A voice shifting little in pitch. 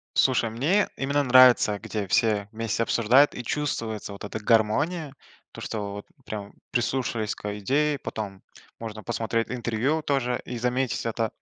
No: average, 3.6 semitones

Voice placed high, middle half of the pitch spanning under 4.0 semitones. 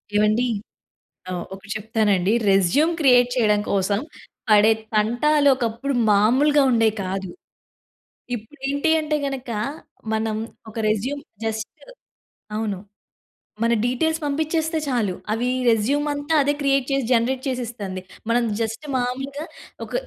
No: high, 240 Hz; average, 4.7 semitones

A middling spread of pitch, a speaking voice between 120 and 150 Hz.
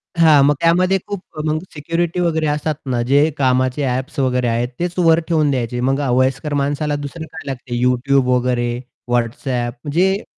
Yes: average, 4.1 semitones; medium, 140 Hz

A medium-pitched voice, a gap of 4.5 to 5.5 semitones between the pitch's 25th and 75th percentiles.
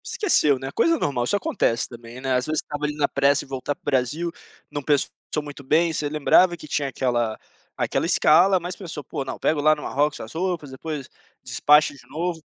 No: medium, 145 Hz; average, 3.3 semitones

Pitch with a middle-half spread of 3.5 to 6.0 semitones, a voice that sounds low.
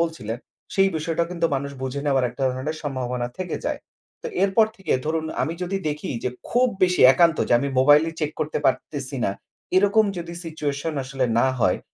No: average, 4.0 semitones; medium, 155 Hz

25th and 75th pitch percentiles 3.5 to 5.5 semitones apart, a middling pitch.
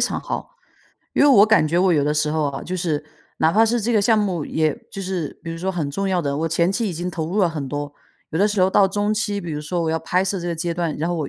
Yes: average, 3.9 semitones; medium, 175 Hz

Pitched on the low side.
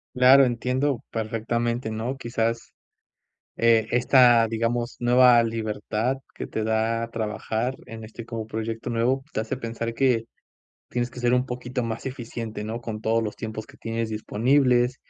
Yes: low, 115 Hz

